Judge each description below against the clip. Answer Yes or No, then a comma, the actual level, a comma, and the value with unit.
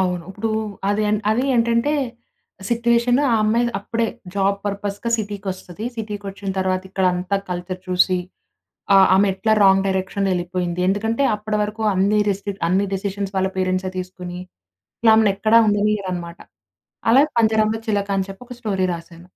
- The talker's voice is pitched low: No, high, 200 Hz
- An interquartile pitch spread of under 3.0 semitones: Yes, narrow, 2.6 semitones